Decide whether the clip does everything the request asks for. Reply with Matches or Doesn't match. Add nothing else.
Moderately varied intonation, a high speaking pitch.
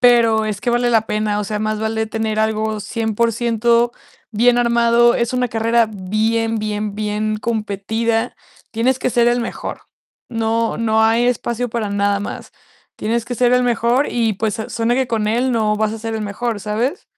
Doesn't match